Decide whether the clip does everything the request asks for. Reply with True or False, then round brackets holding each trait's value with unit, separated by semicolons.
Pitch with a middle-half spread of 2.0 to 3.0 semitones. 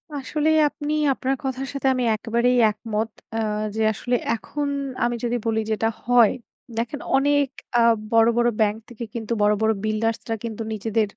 True (2.7 semitones)